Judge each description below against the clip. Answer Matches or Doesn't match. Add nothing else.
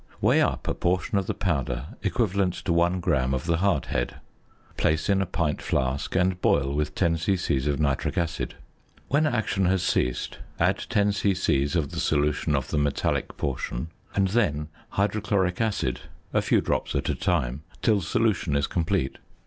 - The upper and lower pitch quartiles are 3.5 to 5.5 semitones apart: Matches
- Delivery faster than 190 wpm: Doesn't match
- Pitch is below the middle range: Matches